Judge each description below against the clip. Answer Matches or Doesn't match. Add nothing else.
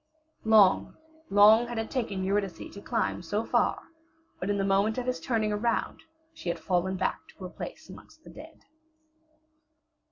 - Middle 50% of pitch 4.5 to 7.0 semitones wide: Doesn't match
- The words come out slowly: Doesn't match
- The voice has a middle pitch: Doesn't match